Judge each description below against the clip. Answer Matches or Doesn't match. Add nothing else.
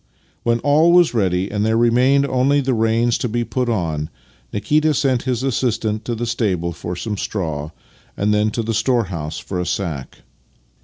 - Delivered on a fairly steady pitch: Doesn't match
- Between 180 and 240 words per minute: Matches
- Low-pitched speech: Matches